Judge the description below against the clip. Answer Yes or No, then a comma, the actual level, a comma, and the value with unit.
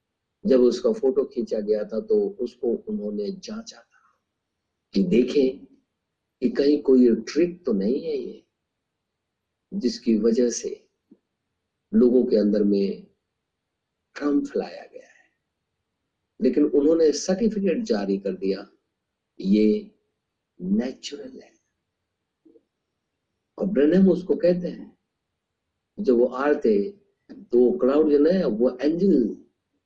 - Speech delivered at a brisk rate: No, slow, 110 wpm